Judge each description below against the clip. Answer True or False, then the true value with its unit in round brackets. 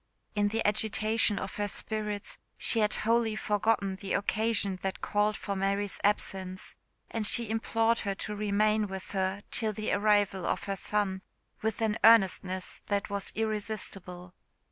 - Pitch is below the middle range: False (205 Hz)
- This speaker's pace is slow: False (150 wpm)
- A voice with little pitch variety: True (1.8 semitones)